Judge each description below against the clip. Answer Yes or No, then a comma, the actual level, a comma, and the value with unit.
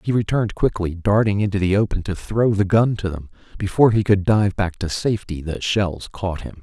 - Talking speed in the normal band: No, fast, 215 wpm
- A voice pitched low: Yes, low, 100 Hz